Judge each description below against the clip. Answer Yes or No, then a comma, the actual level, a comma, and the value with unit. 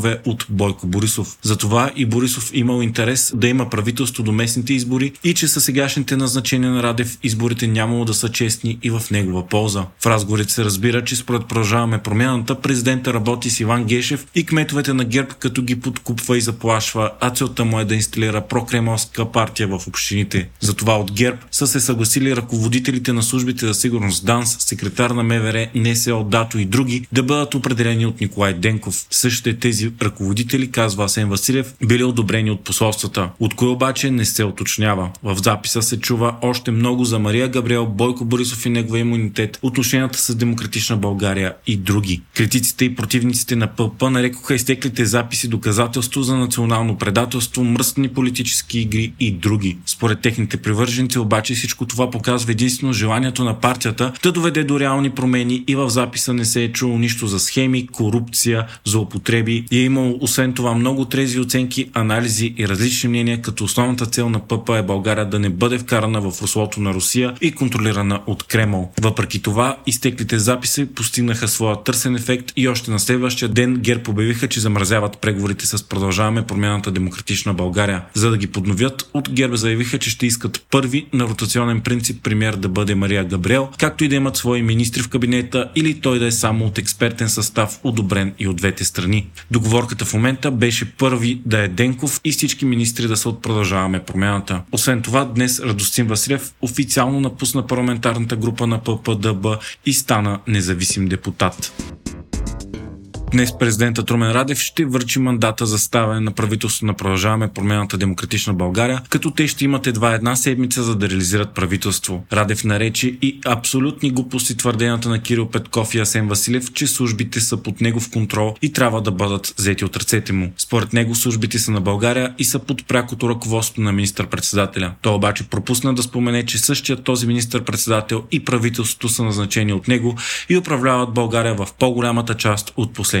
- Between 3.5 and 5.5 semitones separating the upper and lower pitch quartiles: No, average, 2.7 semitones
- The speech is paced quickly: Yes, fast, 175 wpm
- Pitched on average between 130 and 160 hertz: No, low, 120 Hz